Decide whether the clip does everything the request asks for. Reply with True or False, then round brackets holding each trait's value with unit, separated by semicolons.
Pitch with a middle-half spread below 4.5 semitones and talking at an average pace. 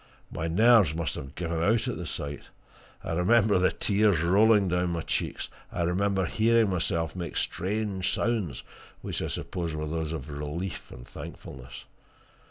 True (4.1 semitones; 160 wpm)